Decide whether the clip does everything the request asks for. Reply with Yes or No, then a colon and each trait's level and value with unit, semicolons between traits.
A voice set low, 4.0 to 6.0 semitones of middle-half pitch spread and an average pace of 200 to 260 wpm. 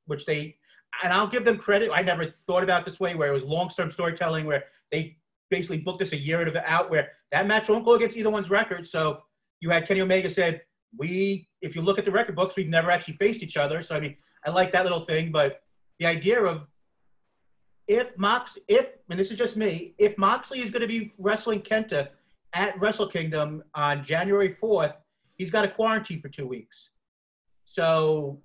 No: medium, 180 Hz; average, 4.5 semitones; fast, 205 wpm